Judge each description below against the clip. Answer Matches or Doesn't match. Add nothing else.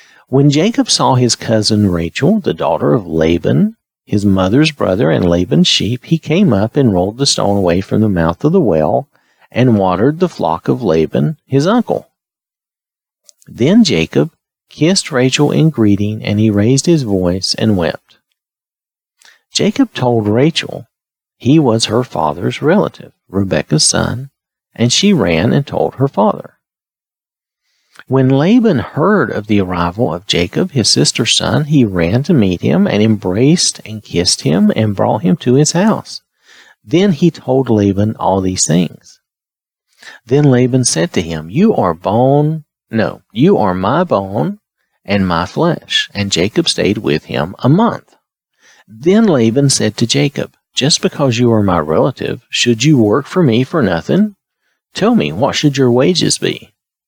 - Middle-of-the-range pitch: Doesn't match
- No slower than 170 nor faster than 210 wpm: Doesn't match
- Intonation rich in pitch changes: Matches